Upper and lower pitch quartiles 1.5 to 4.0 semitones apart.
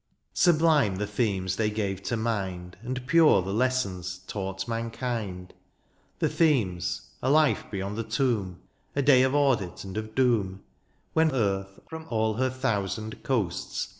No: average, 5.0 semitones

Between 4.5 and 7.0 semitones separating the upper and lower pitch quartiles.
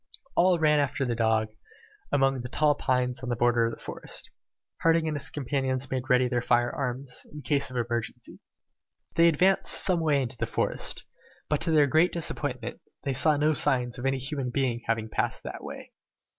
No: average, 3.5 semitones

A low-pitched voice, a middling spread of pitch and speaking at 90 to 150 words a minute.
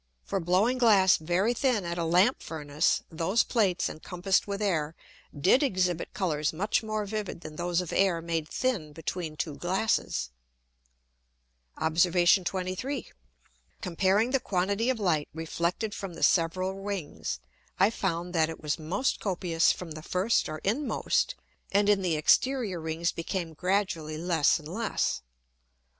No: medium, 180 Hz; average, 3.7 semitones; average, 145 wpm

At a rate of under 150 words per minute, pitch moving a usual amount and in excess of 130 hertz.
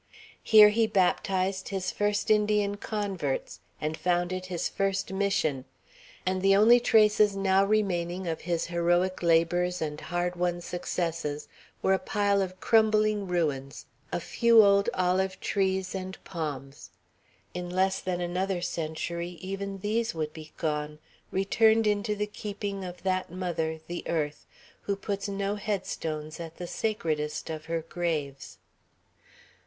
Yes: average, 140 wpm; average, 3.1 semitones; medium, 185 Hz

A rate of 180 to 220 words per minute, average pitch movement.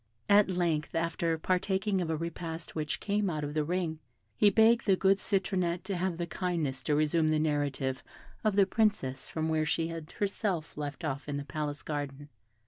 Yes: average, 190 wpm; average, 4.0 semitones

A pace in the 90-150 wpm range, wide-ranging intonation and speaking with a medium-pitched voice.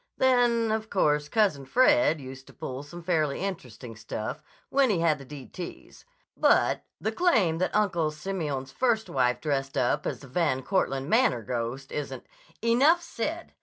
No: average, 165 wpm; wide, 8.5 semitones; medium, 160 Hz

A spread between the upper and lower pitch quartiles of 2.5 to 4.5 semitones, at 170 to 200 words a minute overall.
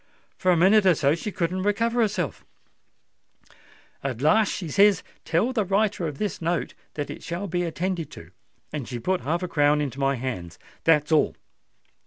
No: average, 5.0 semitones; average, 175 wpm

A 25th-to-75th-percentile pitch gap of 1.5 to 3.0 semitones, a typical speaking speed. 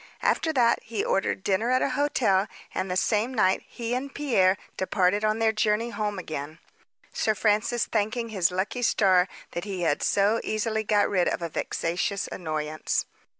No: average, 3.5 semitones; average, 170 wpm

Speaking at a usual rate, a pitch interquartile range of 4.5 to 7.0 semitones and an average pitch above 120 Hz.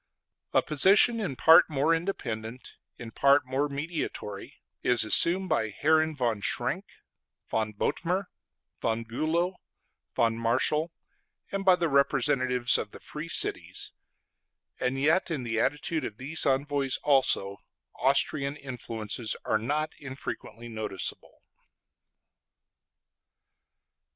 No: slow, 110 wpm; wide, 5.4 semitones; medium, 140 Hz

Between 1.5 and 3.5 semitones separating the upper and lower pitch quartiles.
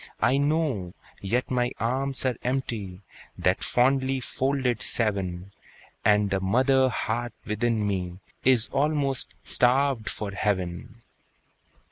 No: average, 4.5 semitones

